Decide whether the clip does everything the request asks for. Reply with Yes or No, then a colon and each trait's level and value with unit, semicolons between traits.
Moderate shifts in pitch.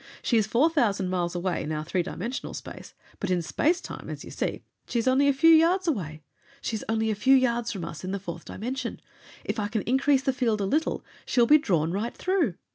No: wide, 6.3 semitones